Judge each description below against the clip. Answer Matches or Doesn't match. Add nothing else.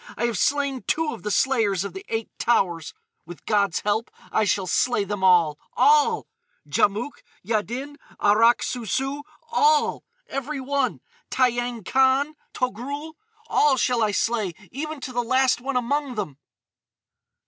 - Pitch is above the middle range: Matches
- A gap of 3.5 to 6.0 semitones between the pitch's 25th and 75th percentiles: Matches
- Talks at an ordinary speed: Doesn't match